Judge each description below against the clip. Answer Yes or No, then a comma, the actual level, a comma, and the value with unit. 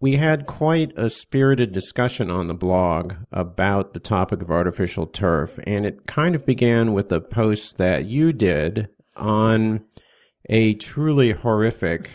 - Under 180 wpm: Yes, average, 150 wpm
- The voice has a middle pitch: No, low, 110 Hz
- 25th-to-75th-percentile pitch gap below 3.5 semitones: No, average, 5.3 semitones